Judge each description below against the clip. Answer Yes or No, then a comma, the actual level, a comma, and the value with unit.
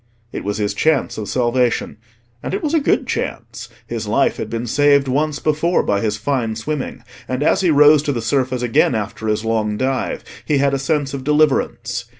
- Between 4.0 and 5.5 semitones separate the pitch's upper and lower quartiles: Yes, average, 4.6 semitones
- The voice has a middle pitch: No, low, 130 Hz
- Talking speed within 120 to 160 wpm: No, average, 200 wpm